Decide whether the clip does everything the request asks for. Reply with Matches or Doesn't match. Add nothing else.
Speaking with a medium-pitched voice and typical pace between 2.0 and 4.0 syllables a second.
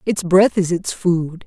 Matches